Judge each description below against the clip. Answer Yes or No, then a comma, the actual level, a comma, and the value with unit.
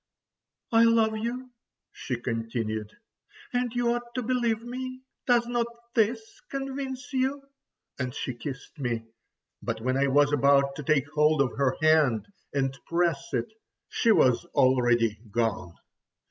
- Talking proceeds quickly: No, slow, 135 wpm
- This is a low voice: No, medium, 155 Hz